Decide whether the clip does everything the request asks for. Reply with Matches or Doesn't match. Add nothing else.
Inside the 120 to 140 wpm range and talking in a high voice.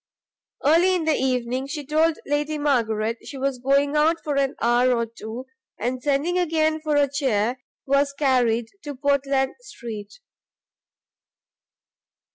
Matches